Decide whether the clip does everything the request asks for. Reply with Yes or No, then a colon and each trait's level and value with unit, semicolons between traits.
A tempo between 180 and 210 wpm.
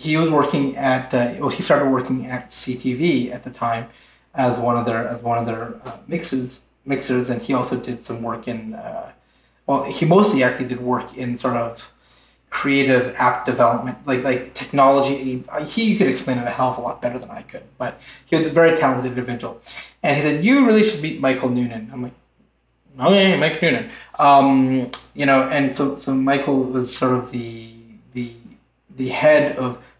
Yes: average, 195 wpm